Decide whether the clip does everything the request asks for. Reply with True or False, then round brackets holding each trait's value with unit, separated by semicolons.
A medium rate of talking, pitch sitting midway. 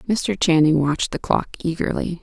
True (160 wpm; 170 Hz)